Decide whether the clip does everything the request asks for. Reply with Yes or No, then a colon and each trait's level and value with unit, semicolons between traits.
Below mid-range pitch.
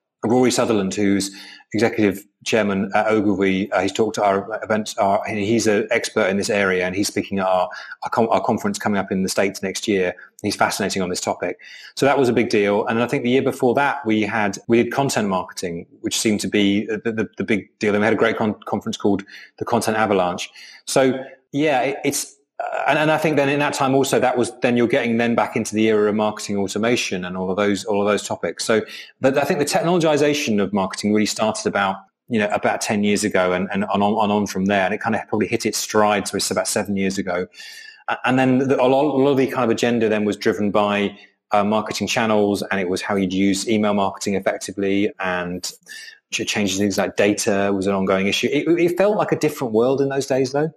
Yes: low, 105 Hz